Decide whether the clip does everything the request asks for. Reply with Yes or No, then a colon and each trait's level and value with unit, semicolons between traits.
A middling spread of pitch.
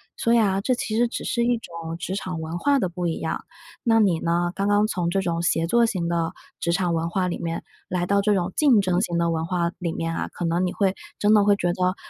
Yes: average, 3.3 semitones